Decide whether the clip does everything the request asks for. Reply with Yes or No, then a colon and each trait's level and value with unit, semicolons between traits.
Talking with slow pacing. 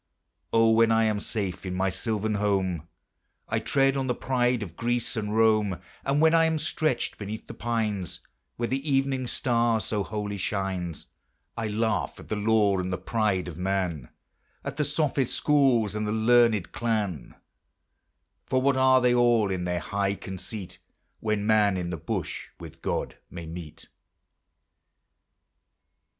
No: average, 160 wpm